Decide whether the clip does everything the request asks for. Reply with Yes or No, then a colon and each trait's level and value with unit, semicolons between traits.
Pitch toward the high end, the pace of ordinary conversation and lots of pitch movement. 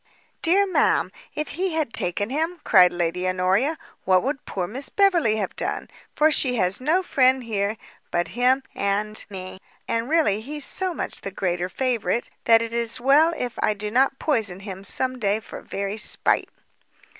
Yes: high, 230 Hz; average, 175 wpm; wide, 6.3 semitones